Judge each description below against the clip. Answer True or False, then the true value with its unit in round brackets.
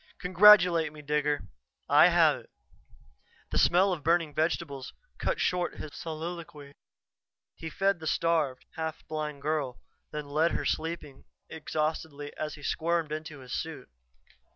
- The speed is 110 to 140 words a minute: True (135 wpm)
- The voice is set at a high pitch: False (155 Hz)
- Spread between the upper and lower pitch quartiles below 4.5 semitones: True (2.4 semitones)